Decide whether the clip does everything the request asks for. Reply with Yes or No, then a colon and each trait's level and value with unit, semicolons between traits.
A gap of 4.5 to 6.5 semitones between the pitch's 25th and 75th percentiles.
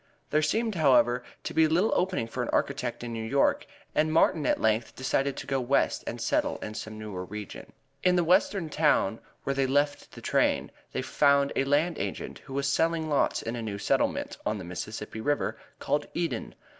Yes: wide, 5.6 semitones